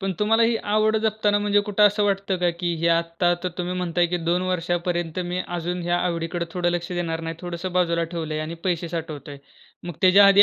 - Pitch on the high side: No, medium, 175 Hz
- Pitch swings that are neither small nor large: No, narrow, 2.3 semitones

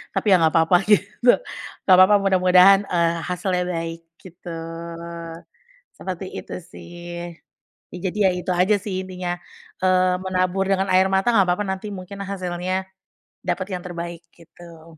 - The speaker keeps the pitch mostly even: Yes, narrow, 1.6 semitones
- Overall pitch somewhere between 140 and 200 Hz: Yes, medium, 185 Hz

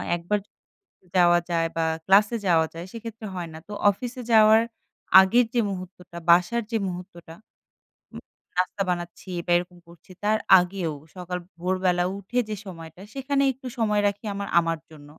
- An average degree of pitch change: Yes, average, 3.6 semitones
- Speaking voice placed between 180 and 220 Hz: Yes, medium, 185 Hz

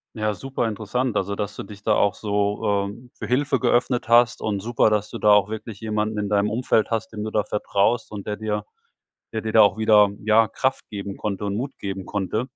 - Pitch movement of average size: No, narrow, 1.8 semitones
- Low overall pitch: Yes, low, 105 Hz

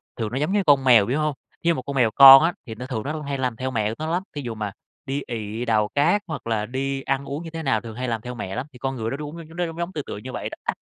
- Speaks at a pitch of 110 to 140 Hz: Yes, low, 135 Hz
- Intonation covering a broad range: No, average, 4.6 semitones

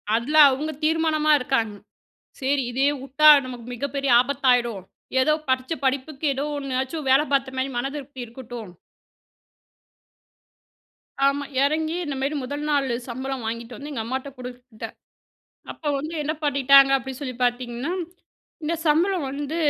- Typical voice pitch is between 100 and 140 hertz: No, very high, 270 Hz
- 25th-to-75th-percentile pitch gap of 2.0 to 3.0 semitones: Yes, narrow, 2.5 semitones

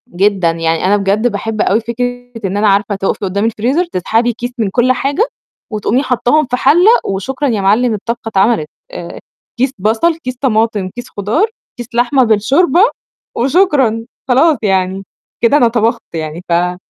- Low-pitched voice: No, high, 230 Hz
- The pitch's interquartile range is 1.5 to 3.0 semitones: No, average, 4.3 semitones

